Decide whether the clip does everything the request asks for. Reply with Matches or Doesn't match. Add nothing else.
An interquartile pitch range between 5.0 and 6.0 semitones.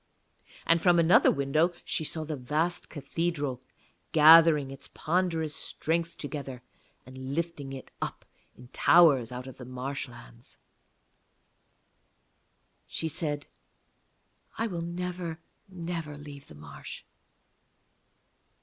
Doesn't match